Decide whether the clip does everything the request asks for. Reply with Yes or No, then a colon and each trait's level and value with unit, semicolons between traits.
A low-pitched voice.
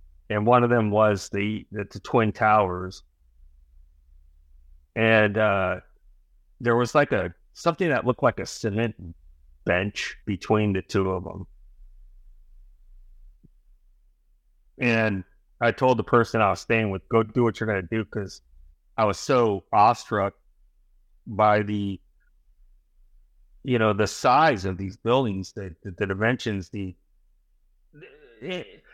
Yes: very low, 95 Hz